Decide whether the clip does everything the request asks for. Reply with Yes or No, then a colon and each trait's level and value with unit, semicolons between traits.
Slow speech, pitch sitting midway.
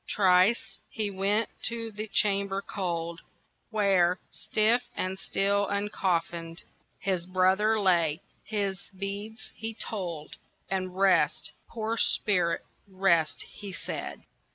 No: slow, 105 wpm; high, 195 Hz